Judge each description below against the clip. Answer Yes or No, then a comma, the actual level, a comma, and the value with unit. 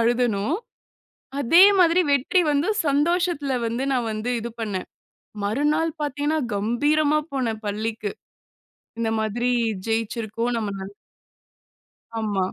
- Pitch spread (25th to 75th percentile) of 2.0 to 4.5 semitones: No, average, 5.1 semitones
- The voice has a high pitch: Yes, high, 240 Hz